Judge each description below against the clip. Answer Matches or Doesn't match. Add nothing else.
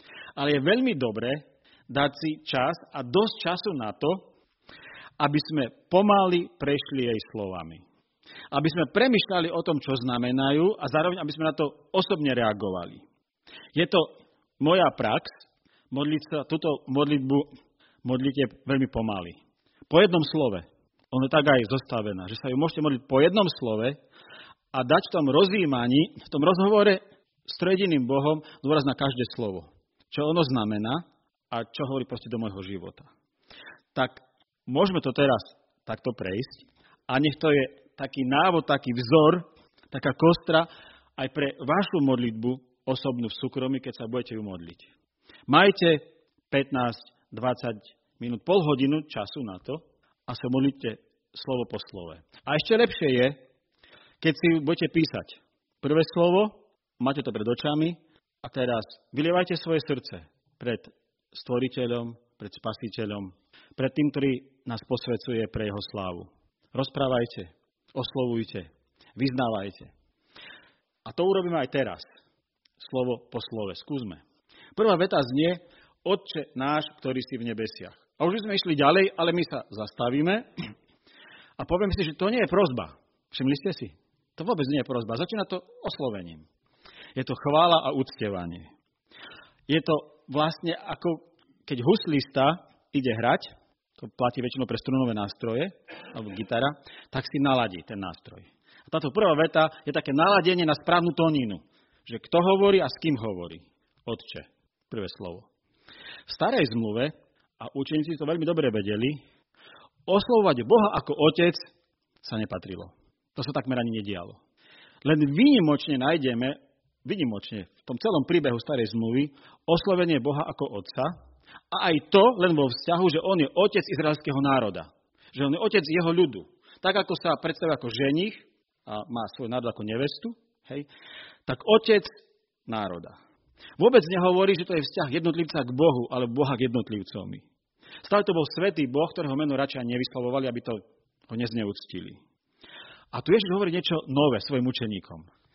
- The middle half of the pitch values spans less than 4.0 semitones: Doesn't match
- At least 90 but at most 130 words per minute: Doesn't match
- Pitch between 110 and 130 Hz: Doesn't match